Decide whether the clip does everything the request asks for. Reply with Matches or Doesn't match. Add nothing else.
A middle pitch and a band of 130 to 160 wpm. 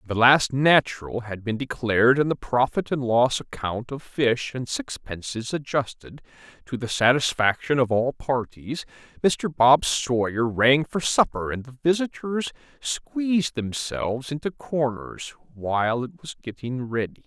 Doesn't match